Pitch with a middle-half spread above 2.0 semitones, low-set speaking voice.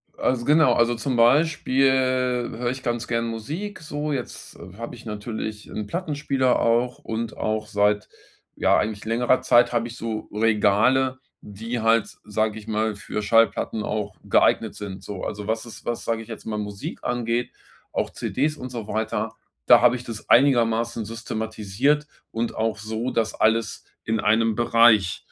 Yes: narrow, 2.4 semitones; low, 115 Hz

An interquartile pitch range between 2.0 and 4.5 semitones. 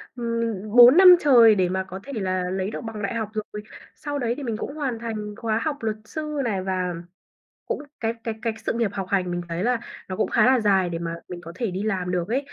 Yes: average, 4.2 semitones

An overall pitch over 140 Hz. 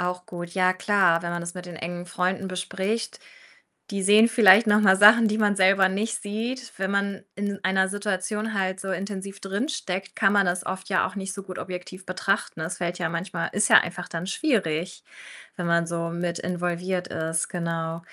Yes: high, 190 Hz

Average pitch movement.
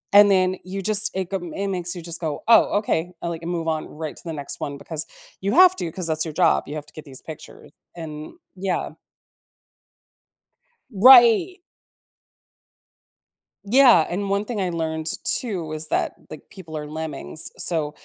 Yes: average, 4.0 semitones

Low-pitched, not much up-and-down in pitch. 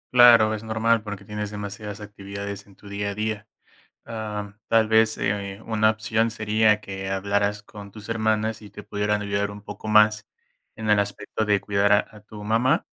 Yes: low, 105 Hz; narrow, 1.3 semitones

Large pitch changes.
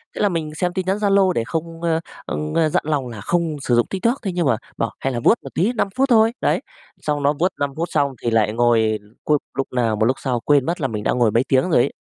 Yes: wide, 6.6 semitones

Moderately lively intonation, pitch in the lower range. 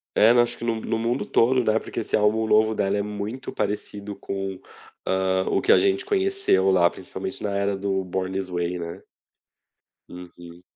Yes: average, 3.0 semitones; low, 100 Hz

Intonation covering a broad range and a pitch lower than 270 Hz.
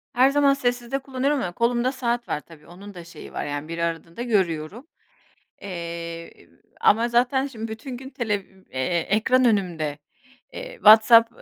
Yes: wide, 6.9 semitones; high, 220 Hz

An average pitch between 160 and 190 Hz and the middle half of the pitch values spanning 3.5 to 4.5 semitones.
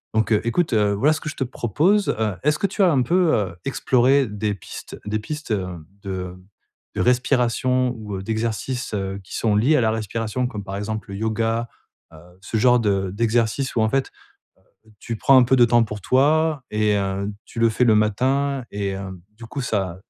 No: low, 115 Hz; average, 3.9 semitones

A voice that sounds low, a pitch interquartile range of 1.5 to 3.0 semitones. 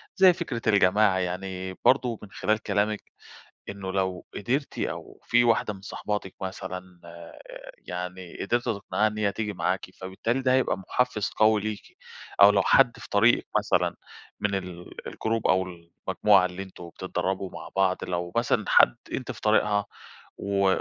Yes: low, 100 Hz; average, 2.7 semitones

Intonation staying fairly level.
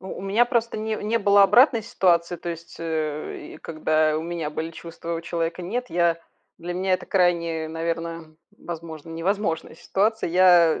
No: average, 3.0 semitones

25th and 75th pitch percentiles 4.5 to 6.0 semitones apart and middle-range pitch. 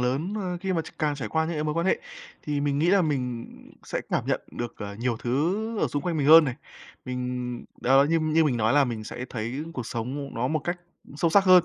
Yes: average, 4.8 semitones; medium, 145 Hz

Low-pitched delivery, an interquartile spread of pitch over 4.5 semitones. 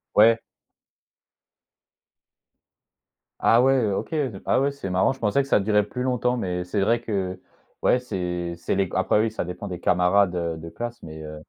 Yes: low, 100 Hz; average, 5.0 semitones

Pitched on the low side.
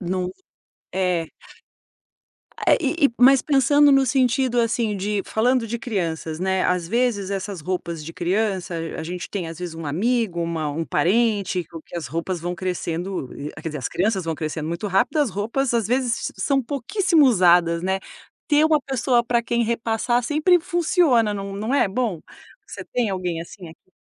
No: high, 205 Hz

